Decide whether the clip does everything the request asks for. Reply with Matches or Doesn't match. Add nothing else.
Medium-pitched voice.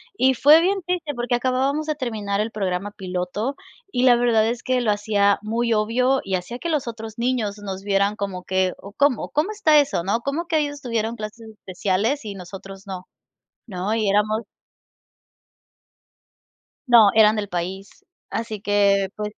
Doesn't match